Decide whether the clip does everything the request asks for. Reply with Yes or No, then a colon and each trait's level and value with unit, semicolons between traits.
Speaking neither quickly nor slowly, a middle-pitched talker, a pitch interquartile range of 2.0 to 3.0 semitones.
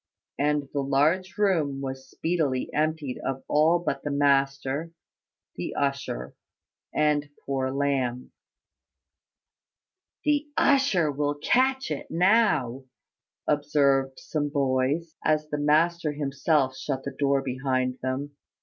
No: slow, 115 wpm; medium, 145 Hz; narrow, 2.5 semitones